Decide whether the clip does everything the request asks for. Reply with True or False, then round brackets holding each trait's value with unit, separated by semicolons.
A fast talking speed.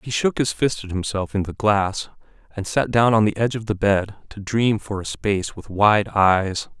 True (230 wpm)